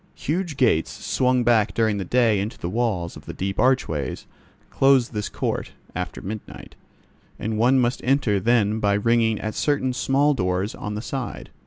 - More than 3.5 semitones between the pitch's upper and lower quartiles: Yes, average, 3.9 semitones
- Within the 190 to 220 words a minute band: No, average, 170 wpm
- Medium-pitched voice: No, low, 110 Hz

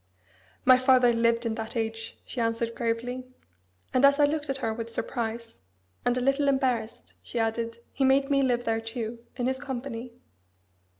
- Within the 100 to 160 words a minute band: No, average, 175 wpm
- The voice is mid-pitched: No, high, 240 Hz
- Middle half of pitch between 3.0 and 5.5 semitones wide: No, narrow, 2.5 semitones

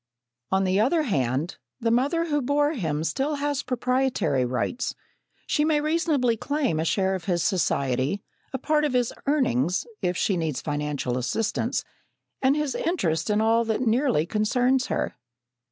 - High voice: Yes, high, 230 Hz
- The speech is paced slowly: No, average, 155 wpm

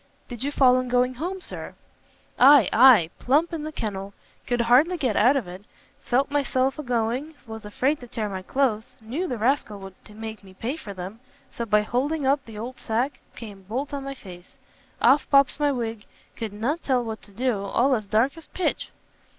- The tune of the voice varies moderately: Yes, average, 4.3 semitones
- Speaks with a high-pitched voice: Yes, high, 245 Hz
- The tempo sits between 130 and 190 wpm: No, average, 200 wpm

